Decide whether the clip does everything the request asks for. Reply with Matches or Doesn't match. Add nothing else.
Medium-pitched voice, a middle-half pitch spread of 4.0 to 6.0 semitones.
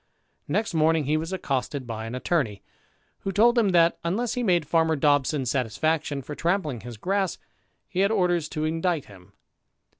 Matches